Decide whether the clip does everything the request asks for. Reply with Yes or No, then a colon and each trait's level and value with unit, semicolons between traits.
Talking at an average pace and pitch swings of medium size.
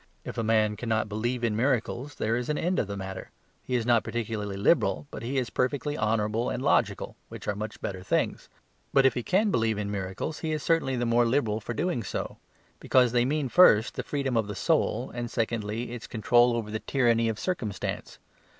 No: fast, 210 wpm; average, 3.2 semitones